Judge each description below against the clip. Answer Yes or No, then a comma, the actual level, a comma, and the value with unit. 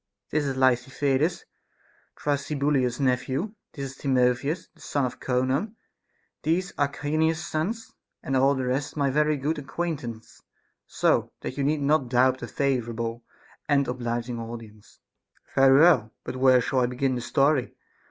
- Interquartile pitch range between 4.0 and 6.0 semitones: No, average, 2.9 semitones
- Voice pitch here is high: No, low, 135 Hz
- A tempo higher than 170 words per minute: No, average, 145 wpm